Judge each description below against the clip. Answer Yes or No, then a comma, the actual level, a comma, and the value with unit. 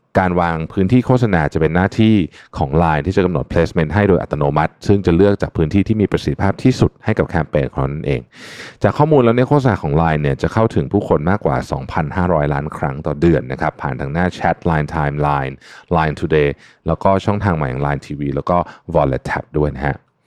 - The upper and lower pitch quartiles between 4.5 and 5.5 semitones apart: Yes, average, 5.0 semitones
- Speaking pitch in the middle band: No, very low, 85 Hz